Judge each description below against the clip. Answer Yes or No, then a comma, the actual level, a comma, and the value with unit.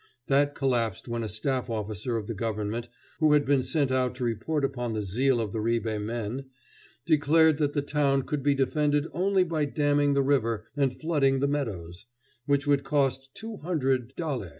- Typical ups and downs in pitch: Yes, average, 3.9 semitones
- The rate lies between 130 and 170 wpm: No, average, 185 wpm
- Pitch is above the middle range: No, low, 135 Hz